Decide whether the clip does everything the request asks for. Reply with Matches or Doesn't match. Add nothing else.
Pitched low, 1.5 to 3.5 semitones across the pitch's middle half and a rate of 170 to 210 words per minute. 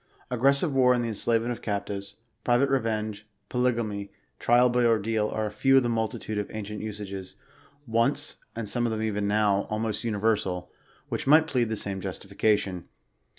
Matches